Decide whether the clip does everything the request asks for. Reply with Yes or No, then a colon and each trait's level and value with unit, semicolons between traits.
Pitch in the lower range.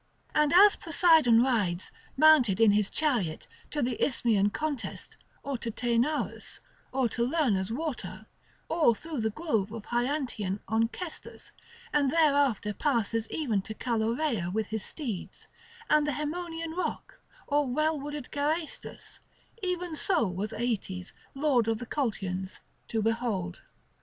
No: high, 245 Hz